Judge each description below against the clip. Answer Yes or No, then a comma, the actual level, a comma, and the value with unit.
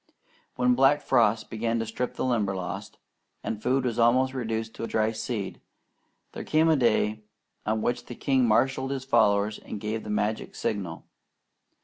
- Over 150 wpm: Yes, average, 160 wpm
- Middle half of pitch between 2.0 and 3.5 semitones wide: Yes, average, 2.9 semitones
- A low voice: Yes, low, 115 Hz